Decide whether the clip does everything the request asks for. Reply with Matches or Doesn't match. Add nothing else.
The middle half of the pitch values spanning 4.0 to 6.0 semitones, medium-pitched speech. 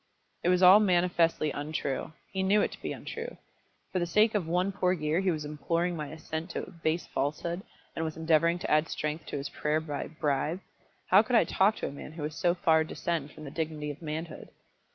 Doesn't match